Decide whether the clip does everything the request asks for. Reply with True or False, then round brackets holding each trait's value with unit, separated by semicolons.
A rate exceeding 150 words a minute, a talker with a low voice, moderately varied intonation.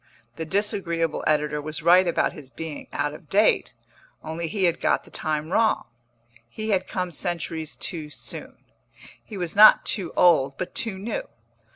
False (165 wpm; 170 Hz; 3.7 semitones)